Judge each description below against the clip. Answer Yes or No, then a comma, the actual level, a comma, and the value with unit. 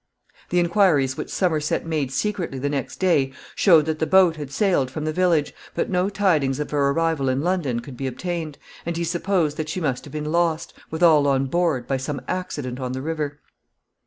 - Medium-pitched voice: Yes, medium, 155 Hz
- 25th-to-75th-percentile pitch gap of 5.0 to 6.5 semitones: No, average, 3.9 semitones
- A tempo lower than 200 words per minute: No, fast, 205 wpm